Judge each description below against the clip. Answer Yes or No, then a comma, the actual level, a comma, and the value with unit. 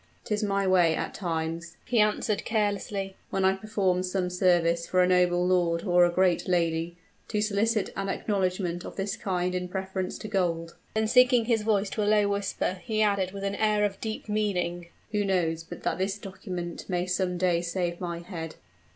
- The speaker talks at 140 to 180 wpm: No, average, 190 wpm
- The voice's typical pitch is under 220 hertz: Yes, medium, 185 Hz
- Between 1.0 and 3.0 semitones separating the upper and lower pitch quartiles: Yes, average, 2.7 semitones